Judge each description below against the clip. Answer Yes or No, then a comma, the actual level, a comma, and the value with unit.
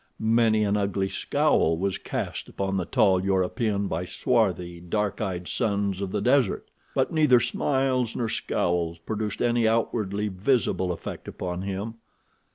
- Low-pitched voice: Yes, low, 100 Hz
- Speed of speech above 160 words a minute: No, average, 145 wpm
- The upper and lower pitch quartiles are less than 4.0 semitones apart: Yes, average, 3.5 semitones